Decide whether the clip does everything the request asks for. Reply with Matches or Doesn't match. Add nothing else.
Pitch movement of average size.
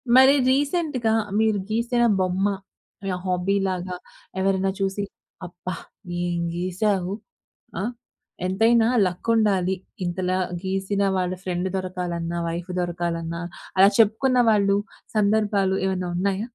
Matches